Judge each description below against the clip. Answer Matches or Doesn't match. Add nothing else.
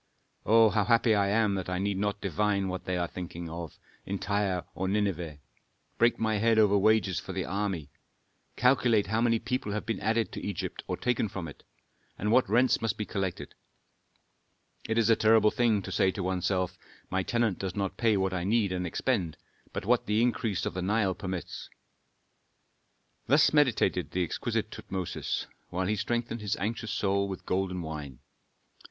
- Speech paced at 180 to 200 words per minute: Matches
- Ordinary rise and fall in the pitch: Matches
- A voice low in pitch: Matches